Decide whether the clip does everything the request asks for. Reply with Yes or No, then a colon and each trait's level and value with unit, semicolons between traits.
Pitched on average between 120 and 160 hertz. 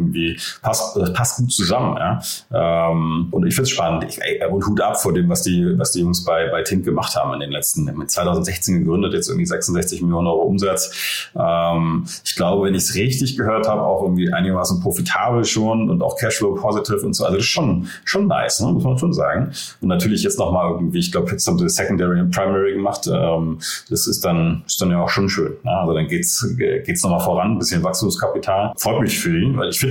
No: low, 100 Hz